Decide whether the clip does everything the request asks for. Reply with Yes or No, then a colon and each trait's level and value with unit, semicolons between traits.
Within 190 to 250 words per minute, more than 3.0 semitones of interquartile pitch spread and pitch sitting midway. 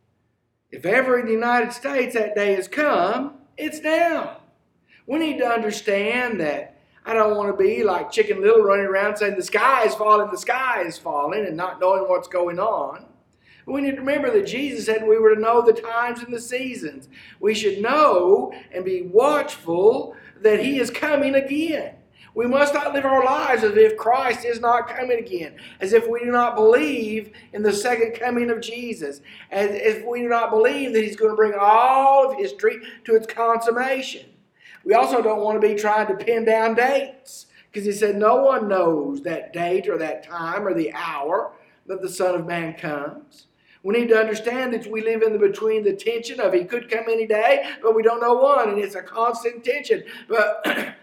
No: average, 200 wpm; average, 4.4 semitones; high, 230 Hz